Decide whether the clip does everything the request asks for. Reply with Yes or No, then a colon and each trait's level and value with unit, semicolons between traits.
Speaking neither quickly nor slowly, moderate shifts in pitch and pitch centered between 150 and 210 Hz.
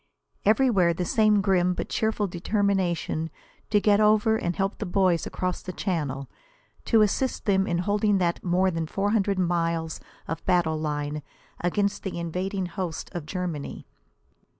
Yes: average, 150 wpm; average, 3.1 semitones; medium, 185 Hz